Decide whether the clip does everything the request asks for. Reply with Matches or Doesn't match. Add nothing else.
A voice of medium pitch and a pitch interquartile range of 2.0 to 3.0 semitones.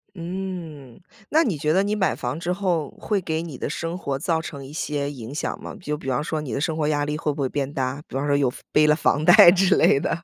Doesn't match